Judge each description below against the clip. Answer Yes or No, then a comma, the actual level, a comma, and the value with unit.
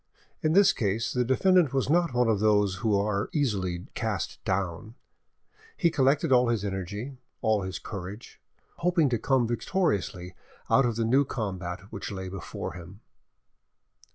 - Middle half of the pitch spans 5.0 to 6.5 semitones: Yes, wide, 5.5 semitones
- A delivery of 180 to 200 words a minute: No, average, 155 wpm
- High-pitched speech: No, low, 110 Hz